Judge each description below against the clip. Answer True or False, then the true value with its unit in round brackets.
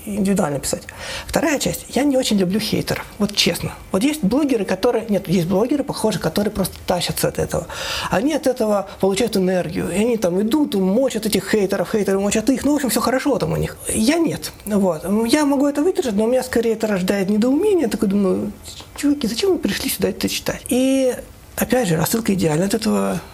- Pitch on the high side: True (220 Hz)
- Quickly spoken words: True (200 wpm)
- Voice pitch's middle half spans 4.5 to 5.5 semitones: True (5.0 semitones)